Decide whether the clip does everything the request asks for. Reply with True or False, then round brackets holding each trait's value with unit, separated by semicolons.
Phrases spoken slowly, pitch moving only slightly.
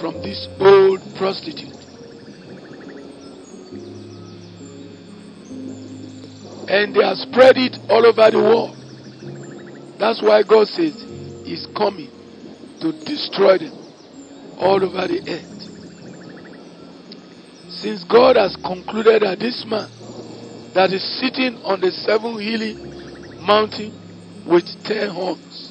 False (100 wpm; 5.5 semitones)